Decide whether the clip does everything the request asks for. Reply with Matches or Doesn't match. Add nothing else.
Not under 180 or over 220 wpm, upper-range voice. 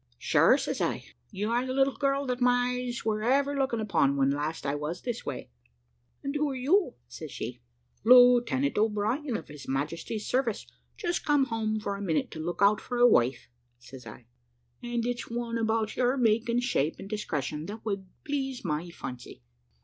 Matches